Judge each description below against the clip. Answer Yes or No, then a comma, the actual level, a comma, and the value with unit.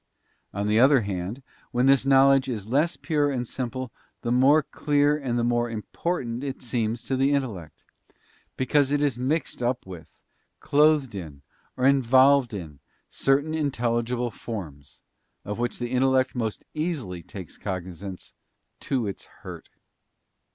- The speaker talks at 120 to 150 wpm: Yes, average, 145 wpm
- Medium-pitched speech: No, low, 125 Hz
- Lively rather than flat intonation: No, average, 4.2 semitones